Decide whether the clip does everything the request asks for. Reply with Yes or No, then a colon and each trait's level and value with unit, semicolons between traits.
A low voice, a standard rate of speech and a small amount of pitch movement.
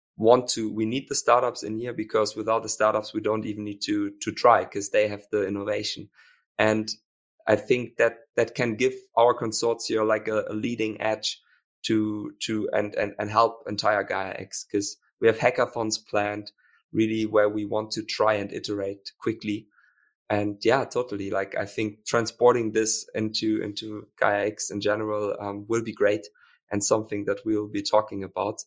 Yes: low, 110 Hz; average, 180 wpm; narrow, 1.4 semitones